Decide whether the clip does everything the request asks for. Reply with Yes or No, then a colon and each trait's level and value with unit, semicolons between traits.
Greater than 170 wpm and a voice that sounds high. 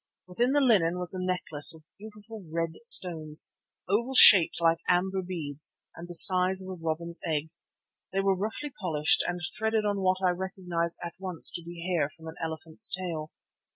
No: average, 185 wpm; medium, 180 Hz